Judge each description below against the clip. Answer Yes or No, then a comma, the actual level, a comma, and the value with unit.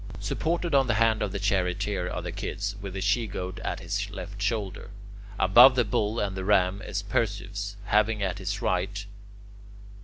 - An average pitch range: No, narrow, 2.3 semitones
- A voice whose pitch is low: Yes, low, 100 Hz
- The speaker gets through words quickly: No, average, 180 wpm